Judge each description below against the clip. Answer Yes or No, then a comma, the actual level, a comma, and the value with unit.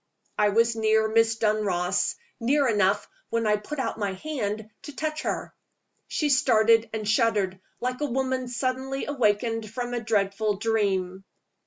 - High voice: Yes, high, 225 Hz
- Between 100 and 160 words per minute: Yes, average, 150 wpm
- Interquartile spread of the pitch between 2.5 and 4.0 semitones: Yes, average, 3.4 semitones